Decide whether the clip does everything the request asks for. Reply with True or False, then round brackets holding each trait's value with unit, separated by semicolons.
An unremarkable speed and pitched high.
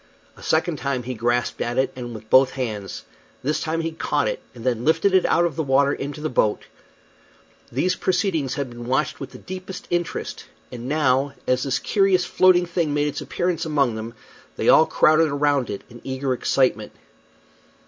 False (190 wpm; 140 Hz)